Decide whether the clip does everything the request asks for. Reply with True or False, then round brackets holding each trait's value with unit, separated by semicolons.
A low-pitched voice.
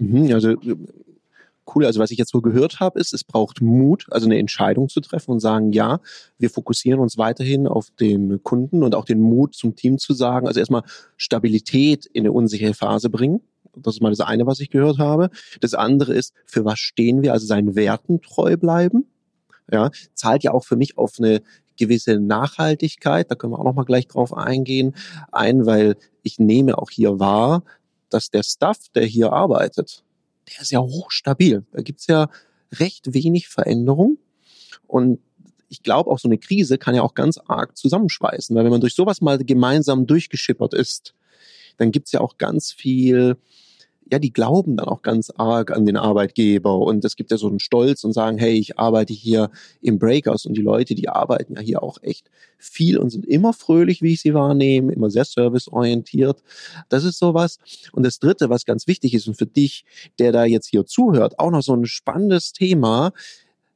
True (125 Hz)